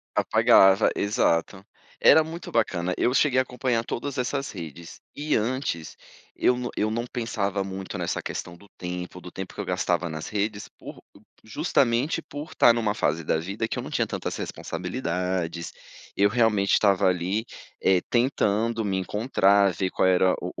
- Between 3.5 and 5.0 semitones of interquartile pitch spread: Yes, average, 4.5 semitones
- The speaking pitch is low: Yes, low, 100 Hz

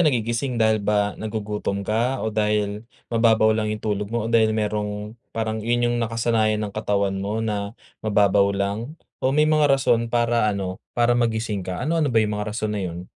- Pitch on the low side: Yes, low, 110 Hz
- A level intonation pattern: Yes, narrow, 2.1 semitones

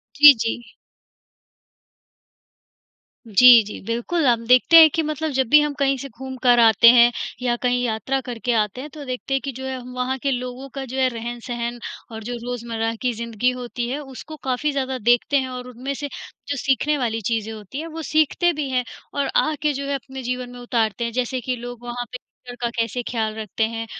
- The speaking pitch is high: Yes, very high, 250 Hz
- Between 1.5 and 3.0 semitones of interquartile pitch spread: Yes, narrow, 2.4 semitones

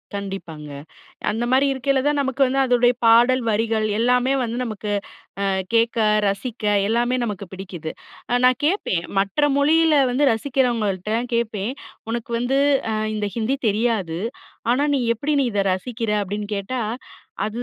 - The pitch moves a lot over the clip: No, average, 3.7 semitones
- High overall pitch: Yes, high, 235 Hz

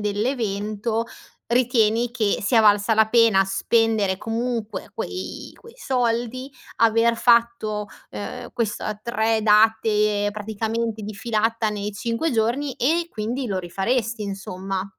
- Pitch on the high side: Yes, high, 220 Hz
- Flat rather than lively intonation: Yes, narrow, 2.1 semitones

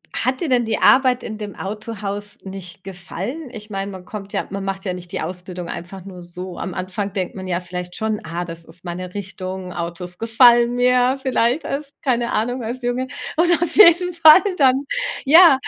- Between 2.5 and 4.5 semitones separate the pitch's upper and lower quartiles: No, wide, 5.6 semitones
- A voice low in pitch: No, high, 205 Hz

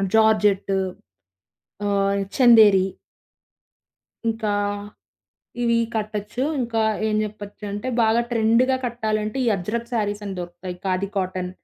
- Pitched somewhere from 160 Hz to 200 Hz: No, high, 210 Hz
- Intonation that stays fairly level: Yes, narrow, 2.3 semitones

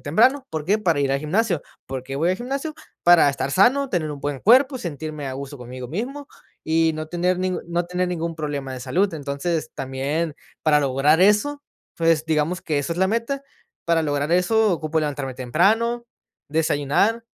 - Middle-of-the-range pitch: Yes, medium, 165 Hz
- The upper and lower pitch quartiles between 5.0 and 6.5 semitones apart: Yes, wide, 5.5 semitones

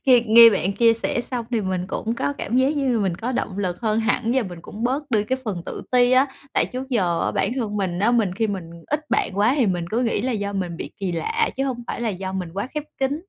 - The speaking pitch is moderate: No, high, 225 Hz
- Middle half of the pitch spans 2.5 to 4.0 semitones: No, average, 4.5 semitones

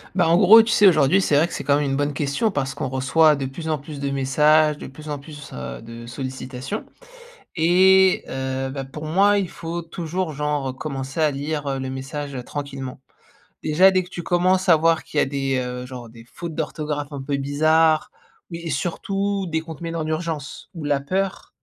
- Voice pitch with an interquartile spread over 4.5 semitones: No, average, 3.5 semitones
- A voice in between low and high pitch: Yes, medium, 150 Hz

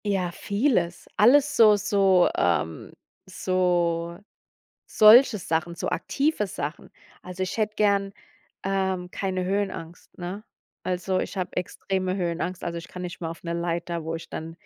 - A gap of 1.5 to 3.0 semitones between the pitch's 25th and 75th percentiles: Yes, average, 2.7 semitones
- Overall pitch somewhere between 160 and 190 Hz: Yes, medium, 185 Hz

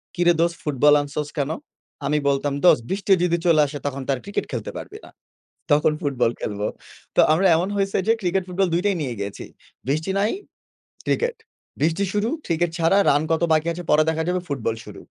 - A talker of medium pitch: Yes, medium, 160 Hz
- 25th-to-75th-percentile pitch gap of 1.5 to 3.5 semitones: No, average, 4.0 semitones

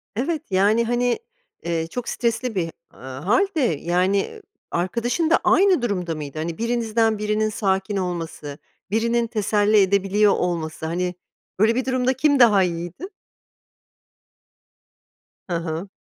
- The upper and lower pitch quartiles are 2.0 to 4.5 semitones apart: No, average, 5.1 semitones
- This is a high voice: Yes, high, 205 Hz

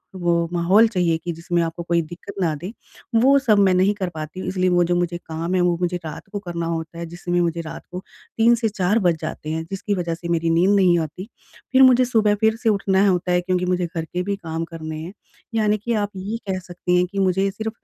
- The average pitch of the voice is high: No, medium, 180 Hz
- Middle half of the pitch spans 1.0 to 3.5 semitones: Yes, average, 2.9 semitones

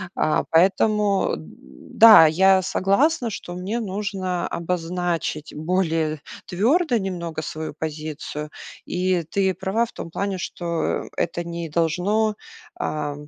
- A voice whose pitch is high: No, medium, 180 Hz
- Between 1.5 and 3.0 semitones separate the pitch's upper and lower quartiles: No, average, 3.5 semitones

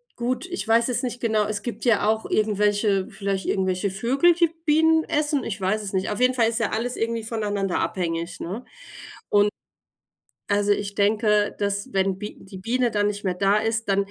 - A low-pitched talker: No, high, 210 Hz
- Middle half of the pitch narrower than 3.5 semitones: Yes, average, 2.9 semitones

